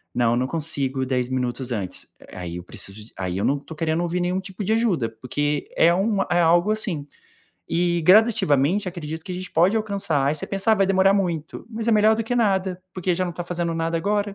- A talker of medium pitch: Yes, medium, 175 Hz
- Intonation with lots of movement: Yes, wide, 5.7 semitones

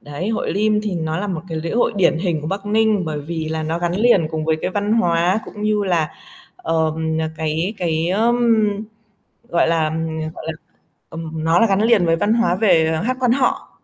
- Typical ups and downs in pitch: Yes, average, 4.9 semitones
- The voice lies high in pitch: No, medium, 175 Hz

